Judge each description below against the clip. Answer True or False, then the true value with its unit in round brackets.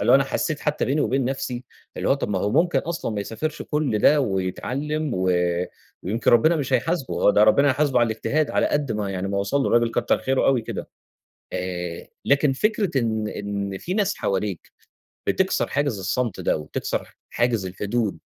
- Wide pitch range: True (5.9 semitones)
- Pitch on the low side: True (120 Hz)